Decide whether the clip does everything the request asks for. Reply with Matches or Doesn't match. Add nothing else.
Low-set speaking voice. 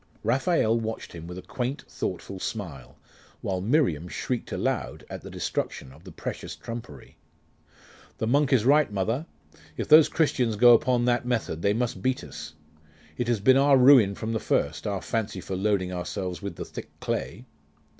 Matches